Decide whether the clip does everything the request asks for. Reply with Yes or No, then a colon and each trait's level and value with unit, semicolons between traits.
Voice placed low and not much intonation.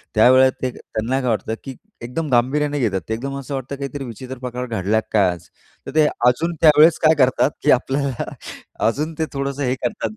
No: low, 130 Hz; average, 3.2 semitones